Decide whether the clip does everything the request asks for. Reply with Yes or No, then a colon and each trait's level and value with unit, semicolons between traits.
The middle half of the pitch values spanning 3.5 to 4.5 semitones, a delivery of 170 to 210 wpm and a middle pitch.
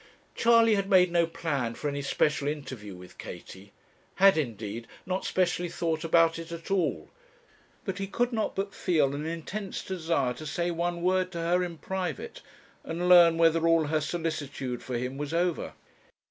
Yes: average, 3.8 semitones; average, 175 wpm; medium, 165 Hz